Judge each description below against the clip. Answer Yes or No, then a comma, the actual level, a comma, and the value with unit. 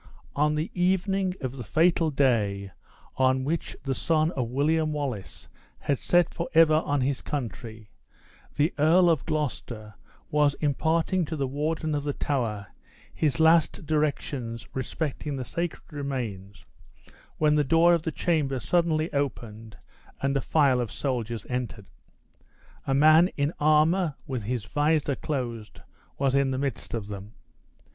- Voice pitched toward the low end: No, medium, 145 Hz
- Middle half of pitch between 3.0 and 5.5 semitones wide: Yes, average, 4.0 semitones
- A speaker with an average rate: Yes, average, 145 wpm